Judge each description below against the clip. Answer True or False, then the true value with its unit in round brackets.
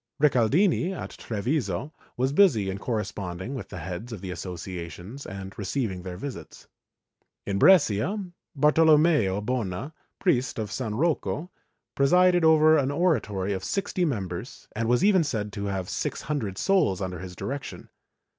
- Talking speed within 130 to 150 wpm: True (145 wpm)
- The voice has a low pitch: True (115 Hz)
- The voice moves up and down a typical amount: False (8.0 semitones)